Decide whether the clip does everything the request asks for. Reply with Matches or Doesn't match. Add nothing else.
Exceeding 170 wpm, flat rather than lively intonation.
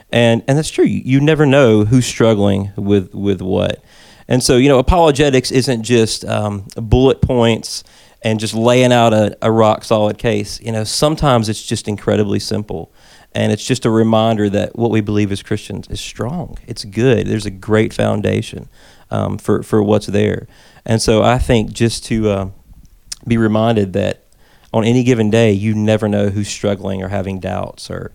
Matches